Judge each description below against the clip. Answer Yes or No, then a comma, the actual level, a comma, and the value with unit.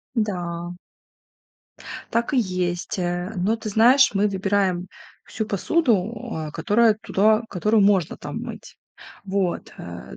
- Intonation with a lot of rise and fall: No, average, 3.7 semitones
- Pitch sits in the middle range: No, high, 195 Hz